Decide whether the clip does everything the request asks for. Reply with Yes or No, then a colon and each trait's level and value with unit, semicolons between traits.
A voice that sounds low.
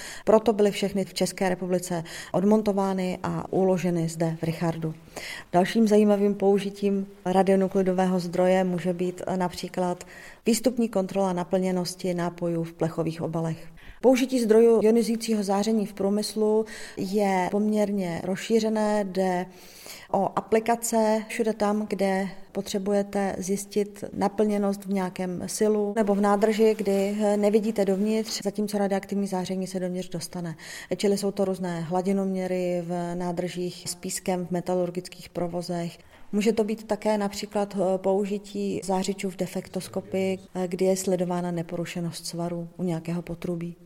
No: high, 190 Hz